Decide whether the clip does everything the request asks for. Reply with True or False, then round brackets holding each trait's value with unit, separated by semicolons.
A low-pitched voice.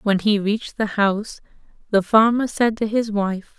False (210 Hz)